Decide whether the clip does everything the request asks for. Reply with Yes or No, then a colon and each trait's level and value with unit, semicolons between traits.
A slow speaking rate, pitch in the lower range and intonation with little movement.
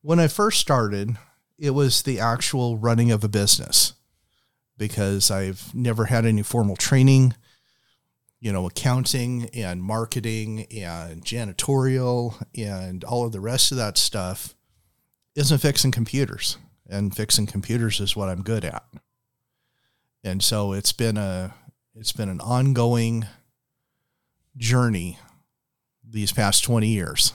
No: slow, 130 wpm; low, 115 Hz; average, 3.6 semitones